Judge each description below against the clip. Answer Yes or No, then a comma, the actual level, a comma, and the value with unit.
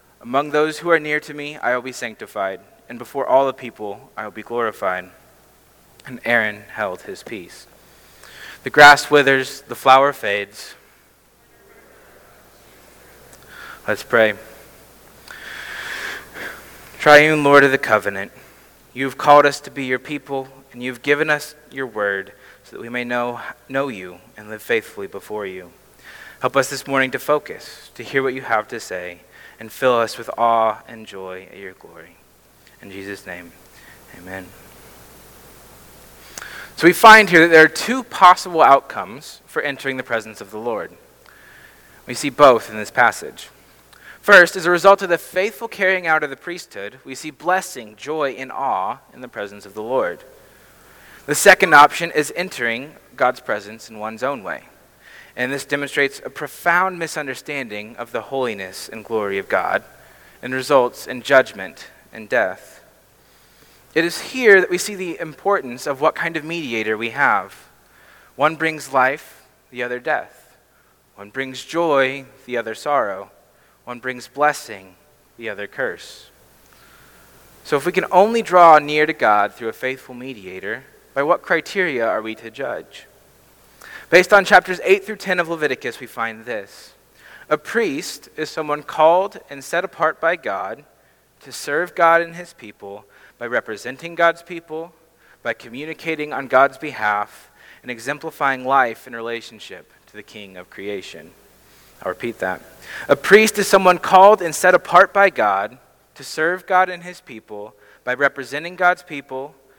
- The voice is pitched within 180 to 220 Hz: No, medium, 140 Hz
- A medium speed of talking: Yes, average, 160 wpm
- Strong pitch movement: Yes, wide, 6.1 semitones